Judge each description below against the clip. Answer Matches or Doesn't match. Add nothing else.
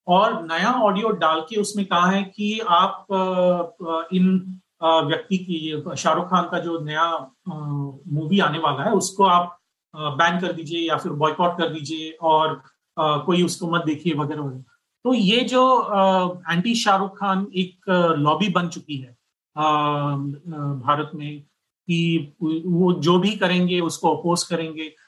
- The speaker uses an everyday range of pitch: Matches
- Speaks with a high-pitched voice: Doesn't match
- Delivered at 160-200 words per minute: Doesn't match